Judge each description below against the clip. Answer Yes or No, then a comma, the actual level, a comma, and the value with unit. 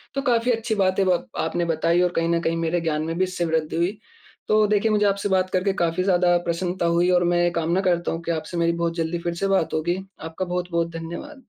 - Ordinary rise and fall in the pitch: No, narrow, 2.2 semitones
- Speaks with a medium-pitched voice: Yes, medium, 175 Hz